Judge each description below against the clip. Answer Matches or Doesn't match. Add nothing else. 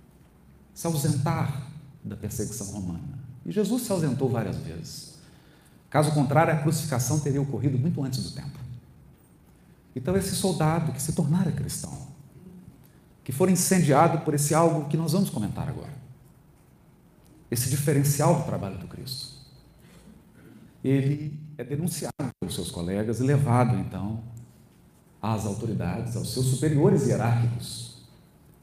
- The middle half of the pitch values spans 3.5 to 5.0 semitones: Matches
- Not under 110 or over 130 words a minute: Matches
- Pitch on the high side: Doesn't match